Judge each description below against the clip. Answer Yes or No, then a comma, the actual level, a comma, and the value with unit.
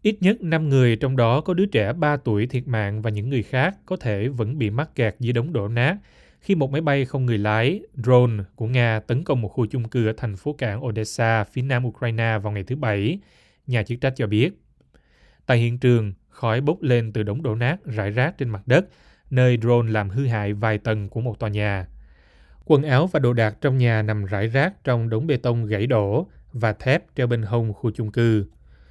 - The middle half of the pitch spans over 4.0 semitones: No, average, 3.4 semitones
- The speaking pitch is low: Yes, low, 120 Hz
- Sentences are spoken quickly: No, average, 230 wpm